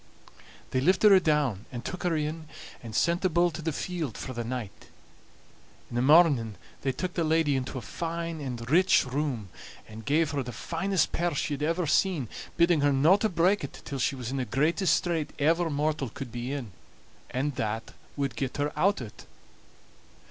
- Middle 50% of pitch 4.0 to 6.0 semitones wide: Yes, average, 4.7 semitones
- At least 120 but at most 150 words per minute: No, average, 195 wpm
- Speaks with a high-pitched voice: No, medium, 150 Hz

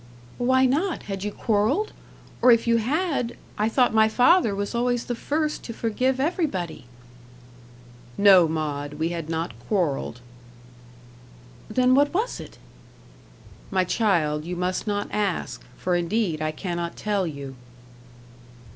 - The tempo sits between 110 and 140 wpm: Yes, slow, 135 wpm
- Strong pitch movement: Yes, wide, 6.5 semitones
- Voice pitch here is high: Yes, high, 210 Hz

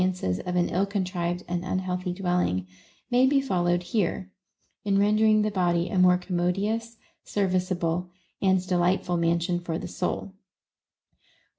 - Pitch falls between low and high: Yes, medium, 180 Hz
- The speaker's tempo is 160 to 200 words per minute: No, average, 140 wpm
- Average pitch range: No, narrow, 2.0 semitones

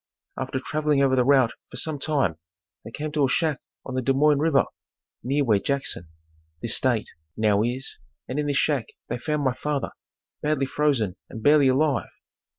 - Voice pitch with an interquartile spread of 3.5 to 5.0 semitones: No, average, 2.8 semitones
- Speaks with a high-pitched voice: No, low, 135 Hz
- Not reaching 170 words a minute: No, average, 180 wpm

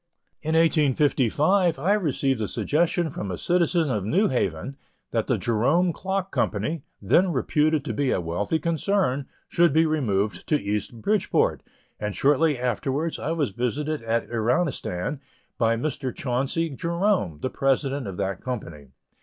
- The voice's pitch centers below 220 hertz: Yes, medium, 140 Hz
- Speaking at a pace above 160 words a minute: No, average, 145 wpm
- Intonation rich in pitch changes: Yes, wide, 6.1 semitones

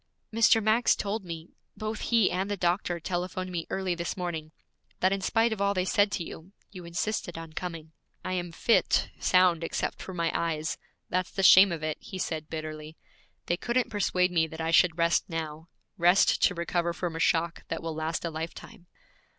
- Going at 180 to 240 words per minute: Yes, average, 195 wpm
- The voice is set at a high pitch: No, medium, 175 Hz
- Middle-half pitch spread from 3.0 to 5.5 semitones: No, narrow, 2.6 semitones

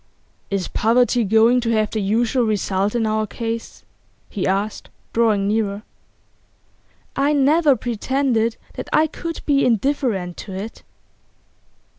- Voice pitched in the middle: No, high, 225 Hz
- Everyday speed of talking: No, slow, 125 wpm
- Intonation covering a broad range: No, average, 3.3 semitones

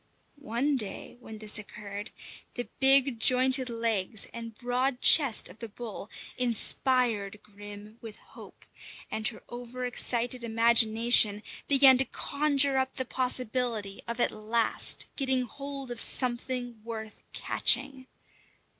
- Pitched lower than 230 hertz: No, high, 240 Hz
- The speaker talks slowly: Yes, slow, 125 wpm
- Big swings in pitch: No, average, 3.0 semitones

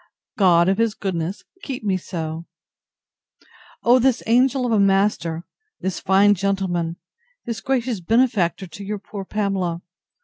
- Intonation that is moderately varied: Yes, average, 4.3 semitones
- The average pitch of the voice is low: No, high, 195 Hz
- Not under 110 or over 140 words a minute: Yes, slow, 135 wpm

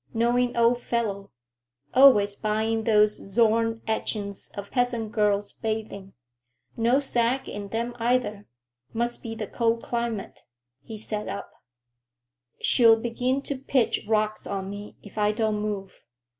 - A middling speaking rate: No, slow, 130 wpm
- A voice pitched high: Yes, high, 225 Hz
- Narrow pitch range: Yes, narrow, 2.2 semitones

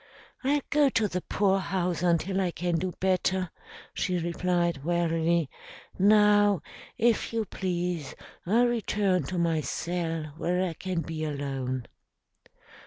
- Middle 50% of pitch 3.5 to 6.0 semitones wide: No, average, 2.8 semitones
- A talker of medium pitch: Yes, medium, 180 Hz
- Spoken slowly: Yes, slow, 125 wpm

